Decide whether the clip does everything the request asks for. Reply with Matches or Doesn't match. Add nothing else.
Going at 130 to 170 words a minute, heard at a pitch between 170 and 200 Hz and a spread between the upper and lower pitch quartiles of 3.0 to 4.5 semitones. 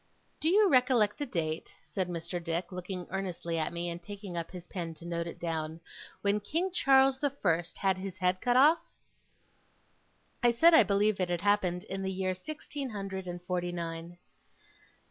Doesn't match